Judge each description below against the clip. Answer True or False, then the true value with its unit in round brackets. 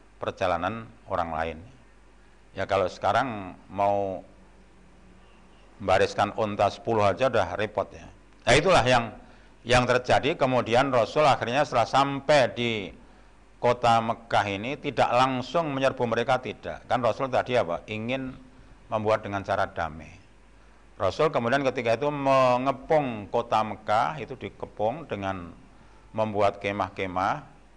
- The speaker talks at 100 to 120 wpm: True (115 wpm)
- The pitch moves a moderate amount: True (4.5 semitones)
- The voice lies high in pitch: False (110 Hz)